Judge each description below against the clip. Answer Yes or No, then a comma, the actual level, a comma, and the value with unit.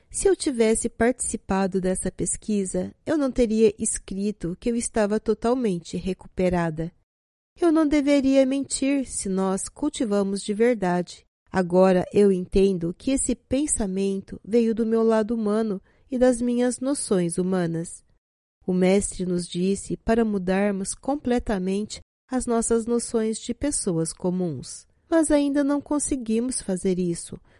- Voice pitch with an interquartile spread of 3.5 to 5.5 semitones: Yes, average, 4.8 semitones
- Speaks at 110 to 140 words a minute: Yes, average, 130 wpm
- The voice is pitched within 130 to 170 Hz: No, high, 215 Hz